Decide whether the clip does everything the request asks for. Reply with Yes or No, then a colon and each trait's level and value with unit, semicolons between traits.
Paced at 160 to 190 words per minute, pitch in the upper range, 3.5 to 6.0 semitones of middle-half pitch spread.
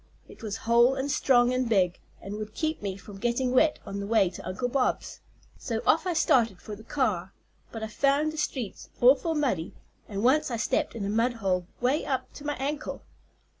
No: fast, 205 wpm; high, 240 Hz; average, 5.0 semitones